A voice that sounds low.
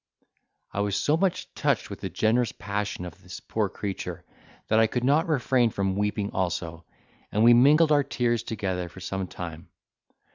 Yes: low, 105 Hz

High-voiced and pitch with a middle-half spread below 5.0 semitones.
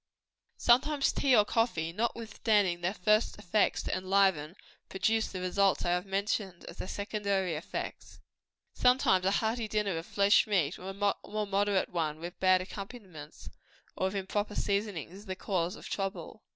Yes: high, 195 Hz; narrow, 2.6 semitones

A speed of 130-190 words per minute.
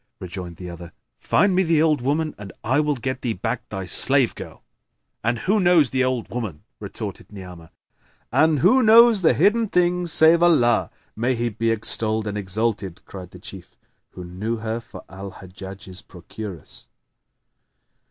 Yes: average, 160 wpm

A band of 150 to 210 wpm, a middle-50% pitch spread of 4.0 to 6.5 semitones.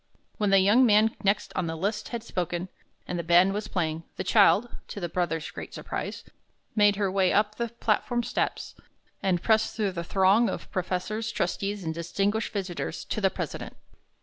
No: average, 180 wpm; average, 3.1 semitones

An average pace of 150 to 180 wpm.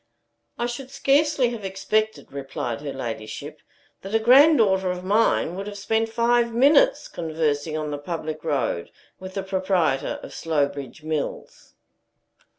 No: average, 140 wpm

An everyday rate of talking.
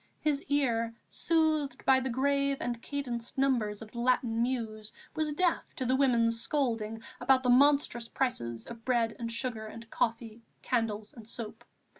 Yes: average, 160 wpm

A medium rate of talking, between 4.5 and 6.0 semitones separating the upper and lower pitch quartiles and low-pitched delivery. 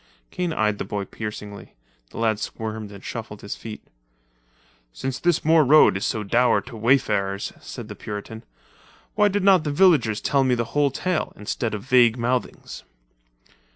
Yes: average, 165 wpm; average, 5.2 semitones; low, 115 Hz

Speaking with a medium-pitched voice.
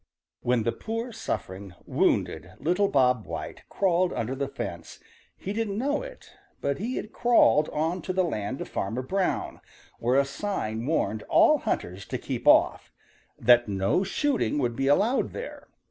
Yes: medium, 145 Hz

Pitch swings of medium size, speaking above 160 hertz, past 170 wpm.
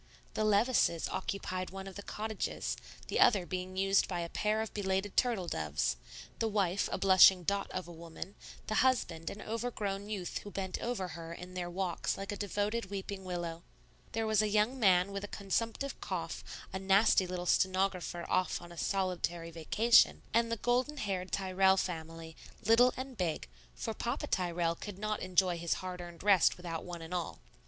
Yes: average, 3.0 semitones; high, 190 Hz; average, 180 wpm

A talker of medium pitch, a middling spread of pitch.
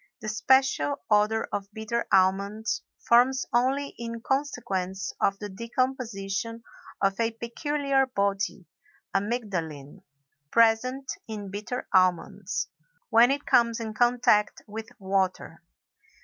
No: high, 220 Hz; average, 3.7 semitones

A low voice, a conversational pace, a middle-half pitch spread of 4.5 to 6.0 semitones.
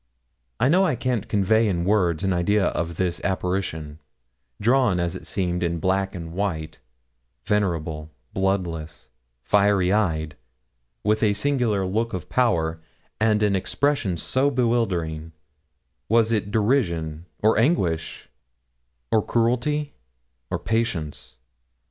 No: very low, 95 Hz; slow, 120 wpm; average, 5.0 semitones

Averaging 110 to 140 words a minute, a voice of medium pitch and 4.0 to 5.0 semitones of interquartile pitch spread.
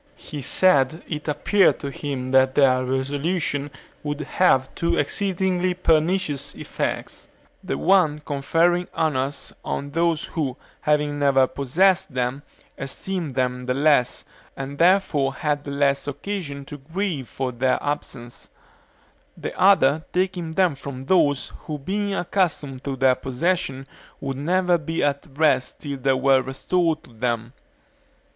Yes: slow, 135 wpm; medium, 145 Hz; average, 4.3 semitones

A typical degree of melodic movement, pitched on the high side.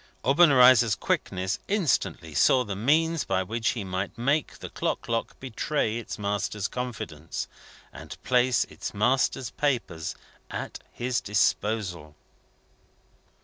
No: average, 4.9 semitones; low, 115 Hz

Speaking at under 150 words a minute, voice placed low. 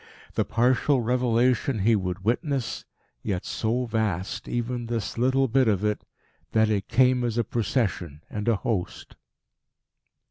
Yes: average, 140 wpm; low, 115 Hz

